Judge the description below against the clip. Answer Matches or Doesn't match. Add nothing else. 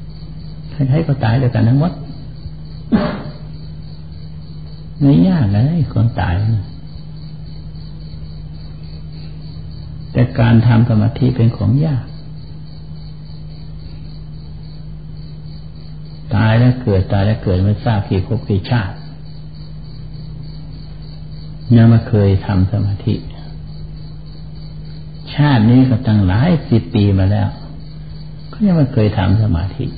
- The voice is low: Matches